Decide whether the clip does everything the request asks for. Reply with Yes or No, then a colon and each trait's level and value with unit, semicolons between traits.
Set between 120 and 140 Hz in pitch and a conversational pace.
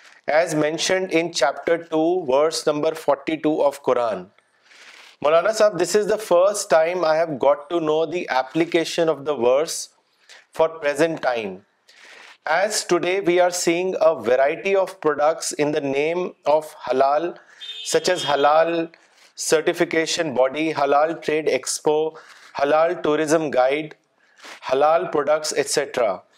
No: medium, 160 Hz; average, 135 wpm